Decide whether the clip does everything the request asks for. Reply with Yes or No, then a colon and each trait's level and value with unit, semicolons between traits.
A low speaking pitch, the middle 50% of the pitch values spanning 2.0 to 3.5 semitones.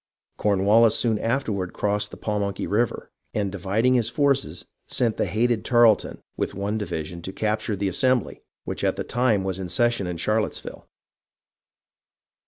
Yes: low, 105 Hz; average, 3.1 semitones